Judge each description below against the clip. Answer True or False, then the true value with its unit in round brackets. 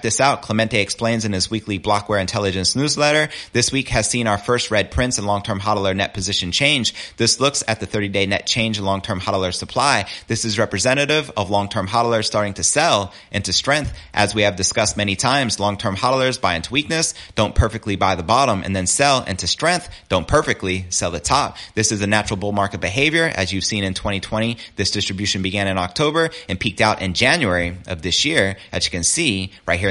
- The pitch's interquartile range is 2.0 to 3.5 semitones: True (3.2 semitones)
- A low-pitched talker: True (105 Hz)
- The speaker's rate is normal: False (215 wpm)